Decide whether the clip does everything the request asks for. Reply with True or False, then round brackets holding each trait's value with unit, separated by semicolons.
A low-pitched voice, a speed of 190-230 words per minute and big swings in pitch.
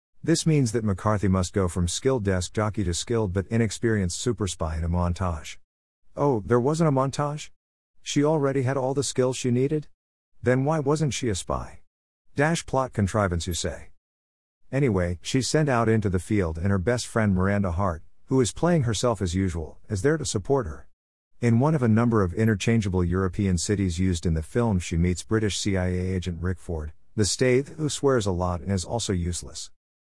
True (100 Hz; 195 wpm; 6.0 semitones)